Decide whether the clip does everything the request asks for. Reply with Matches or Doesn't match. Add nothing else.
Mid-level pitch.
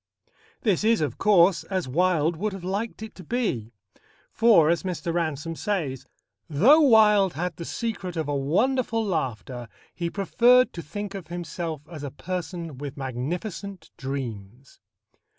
Matches